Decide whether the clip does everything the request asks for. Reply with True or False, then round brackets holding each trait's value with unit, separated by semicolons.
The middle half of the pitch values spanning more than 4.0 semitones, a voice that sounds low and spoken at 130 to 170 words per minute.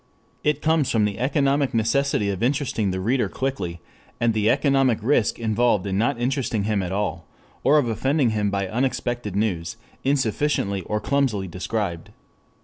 True (5.2 semitones; 115 Hz; 155 wpm)